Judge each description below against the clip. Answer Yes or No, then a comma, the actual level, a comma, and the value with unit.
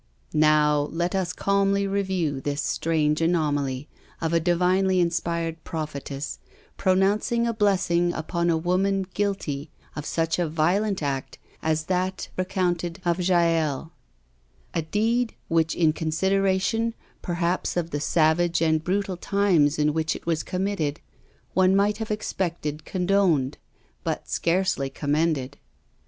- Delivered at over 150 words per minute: No, slow, 135 wpm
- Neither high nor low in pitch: Yes, medium, 170 Hz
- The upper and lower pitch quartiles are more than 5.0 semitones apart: No, average, 3.5 semitones